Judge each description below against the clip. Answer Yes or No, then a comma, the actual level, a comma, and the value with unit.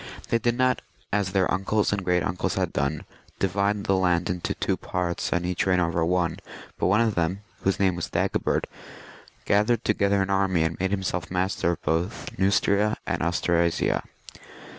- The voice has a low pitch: Yes, very low, 95 Hz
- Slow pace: No, average, 180 wpm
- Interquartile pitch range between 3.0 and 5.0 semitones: No, narrow, 2.5 semitones